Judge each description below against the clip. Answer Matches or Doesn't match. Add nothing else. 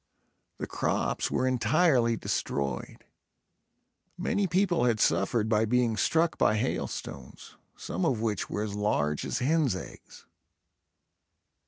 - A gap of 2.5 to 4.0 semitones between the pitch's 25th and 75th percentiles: Doesn't match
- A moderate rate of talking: Doesn't match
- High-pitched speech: Doesn't match